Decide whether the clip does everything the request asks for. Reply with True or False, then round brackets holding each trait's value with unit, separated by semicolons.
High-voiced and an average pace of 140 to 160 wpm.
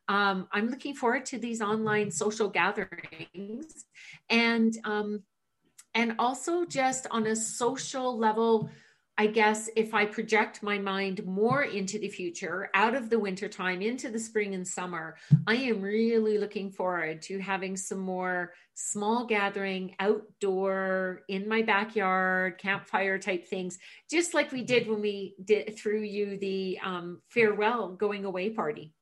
True (210 Hz; 145 wpm)